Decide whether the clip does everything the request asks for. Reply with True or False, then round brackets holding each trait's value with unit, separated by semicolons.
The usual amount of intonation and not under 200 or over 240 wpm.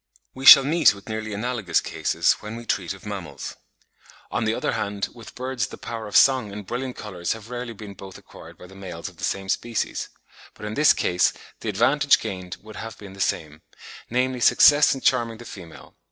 True (3.9 semitones; 205 wpm)